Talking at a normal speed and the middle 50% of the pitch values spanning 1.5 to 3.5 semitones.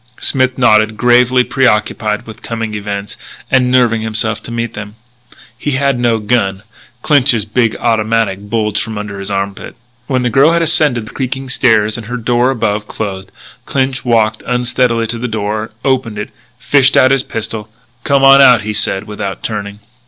Yes: average, 165 wpm; average, 3.0 semitones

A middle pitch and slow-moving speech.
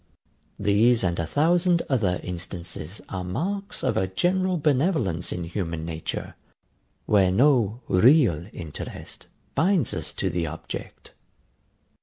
No: low, 100 Hz; slow, 120 wpm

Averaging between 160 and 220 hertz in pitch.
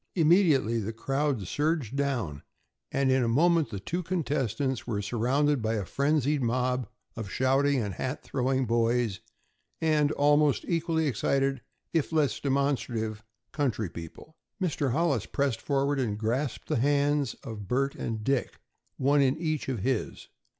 No: low, 135 Hz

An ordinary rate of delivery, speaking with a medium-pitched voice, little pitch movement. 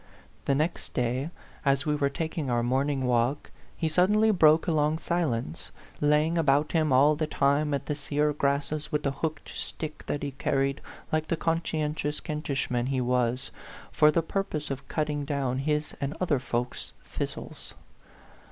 Yes: average, 165 wpm; medium, 150 Hz; narrow, 2.3 semitones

